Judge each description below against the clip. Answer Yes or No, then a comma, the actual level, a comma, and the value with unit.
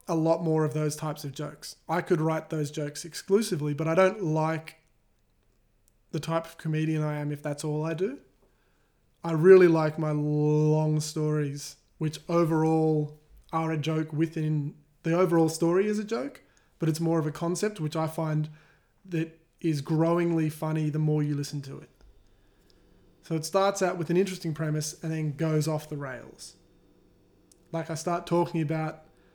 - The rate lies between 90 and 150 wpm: No, average, 175 wpm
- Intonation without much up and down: Yes, narrow, 1.5 semitones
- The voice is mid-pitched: Yes, medium, 160 Hz